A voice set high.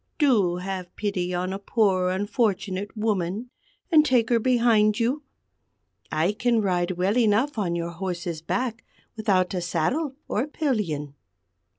Yes: high, 205 Hz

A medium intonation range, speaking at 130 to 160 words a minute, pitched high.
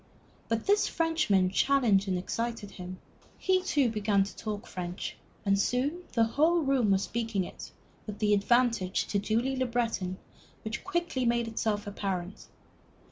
Yes: average, 4.3 semitones; average, 150 wpm; high, 225 Hz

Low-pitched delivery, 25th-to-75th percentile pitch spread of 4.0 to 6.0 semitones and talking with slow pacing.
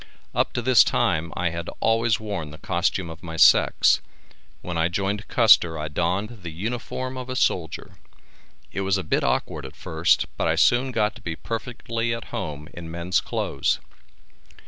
No: very low, 95 Hz; wide, 5.6 semitones; average, 175 wpm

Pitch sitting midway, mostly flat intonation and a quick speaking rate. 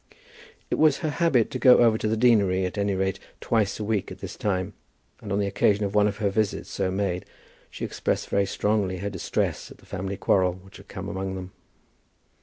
No: low, 100 Hz; narrow, 2.2 semitones; fast, 215 wpm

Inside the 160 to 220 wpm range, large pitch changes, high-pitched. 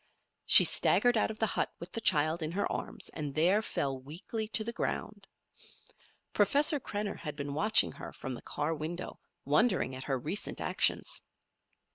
No: average, 170 wpm; wide, 6.7 semitones; medium, 170 Hz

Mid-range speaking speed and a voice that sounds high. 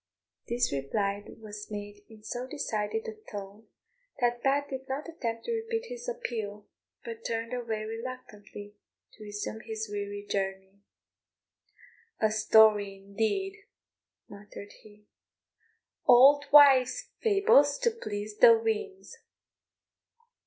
No: slow, 115 wpm; high, 225 Hz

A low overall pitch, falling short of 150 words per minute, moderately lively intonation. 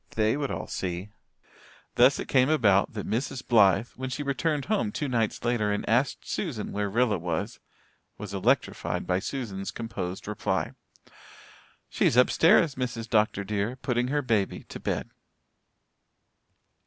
Yes: low, 115 Hz; average, 140 wpm; average, 4.3 semitones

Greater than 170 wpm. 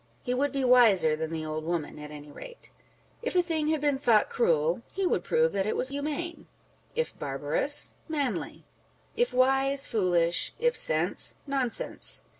No: average, 165 wpm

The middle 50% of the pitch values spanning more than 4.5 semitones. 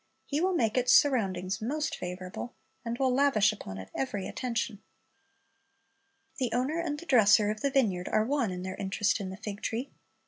Yes: average, 5.3 semitones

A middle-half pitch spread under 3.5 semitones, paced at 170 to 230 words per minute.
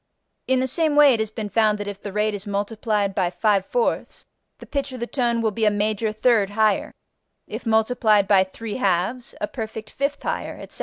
Yes: average, 3.0 semitones; average, 200 wpm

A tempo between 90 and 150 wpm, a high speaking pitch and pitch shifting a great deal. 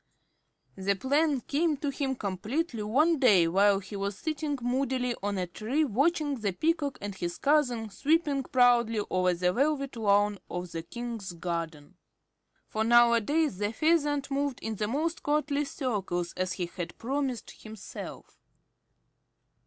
Yes: average, 145 wpm; high, 240 Hz; wide, 6.3 semitones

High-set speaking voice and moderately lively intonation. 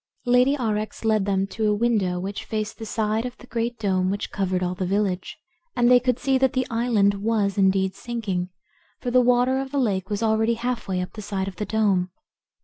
Yes: high, 215 Hz; average, 3.7 semitones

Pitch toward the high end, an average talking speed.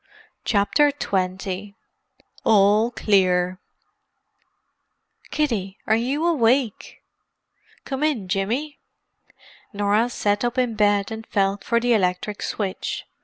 No: high, 210 Hz; slow, 100 wpm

